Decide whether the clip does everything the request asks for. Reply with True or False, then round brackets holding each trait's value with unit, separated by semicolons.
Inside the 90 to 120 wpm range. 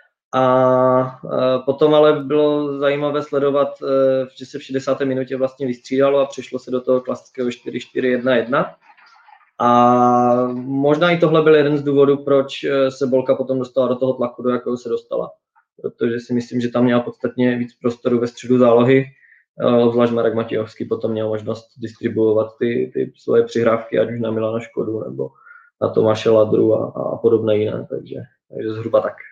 False (160 wpm)